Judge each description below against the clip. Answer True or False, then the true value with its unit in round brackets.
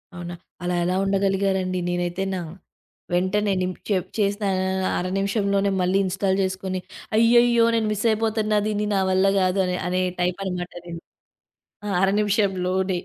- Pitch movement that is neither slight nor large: False (2.0 semitones)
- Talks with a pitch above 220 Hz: False (190 Hz)